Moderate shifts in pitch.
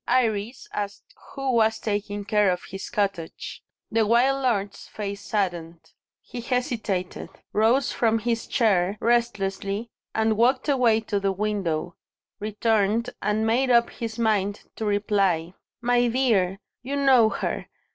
Yes: average, 3.0 semitones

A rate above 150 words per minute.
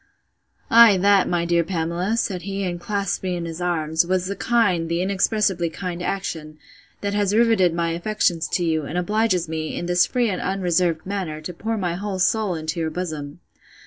Yes: average, 190 wpm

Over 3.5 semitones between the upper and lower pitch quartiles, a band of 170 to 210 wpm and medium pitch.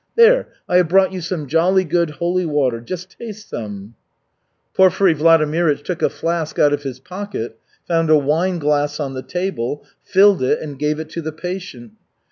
Yes: average, 4.0 semitones; average, 180 wpm; medium, 165 Hz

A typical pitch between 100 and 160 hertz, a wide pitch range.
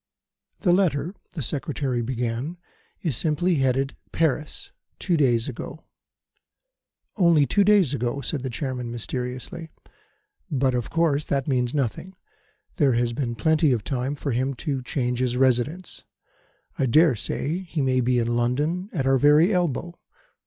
No: low, 135 Hz; average, 4.5 semitones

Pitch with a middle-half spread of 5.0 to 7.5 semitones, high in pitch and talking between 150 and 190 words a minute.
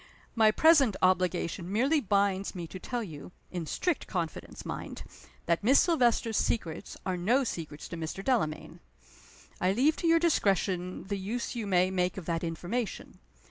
Yes: average, 5.3 semitones; high, 195 Hz; average, 160 wpm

